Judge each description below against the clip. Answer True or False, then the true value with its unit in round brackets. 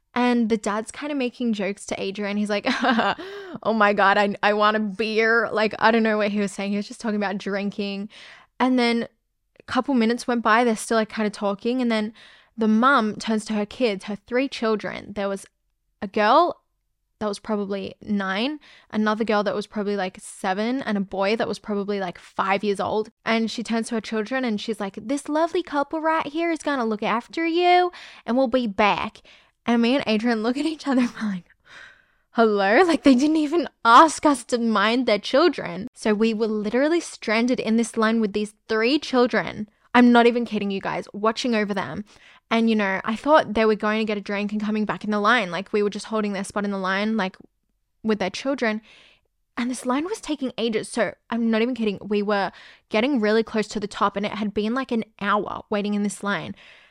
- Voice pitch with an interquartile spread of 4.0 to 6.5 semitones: False (3.0 semitones)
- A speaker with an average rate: False (220 wpm)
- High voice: True (220 Hz)